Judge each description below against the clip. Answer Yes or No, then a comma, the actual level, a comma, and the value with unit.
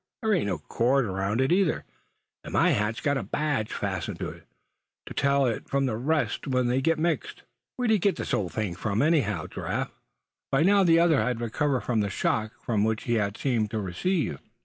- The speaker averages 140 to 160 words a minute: No, average, 200 wpm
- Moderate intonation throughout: No, wide, 6.2 semitones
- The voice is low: Yes, low, 125 Hz